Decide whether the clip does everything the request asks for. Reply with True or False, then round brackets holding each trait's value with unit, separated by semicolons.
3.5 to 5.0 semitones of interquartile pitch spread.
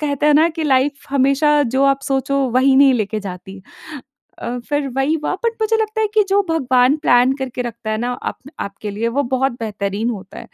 True (3.9 semitones)